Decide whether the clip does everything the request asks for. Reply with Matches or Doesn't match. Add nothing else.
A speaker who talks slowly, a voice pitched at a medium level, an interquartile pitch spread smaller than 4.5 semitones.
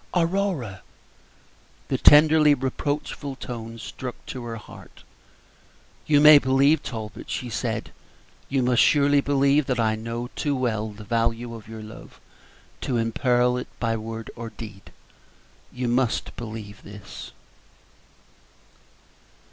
Doesn't match